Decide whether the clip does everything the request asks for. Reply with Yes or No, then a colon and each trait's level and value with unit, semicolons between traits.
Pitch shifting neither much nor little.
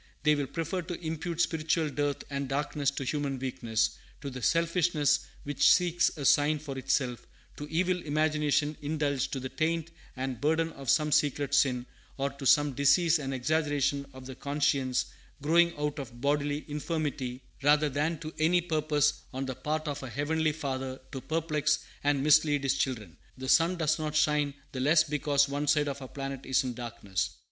No: narrow, 2.3 semitones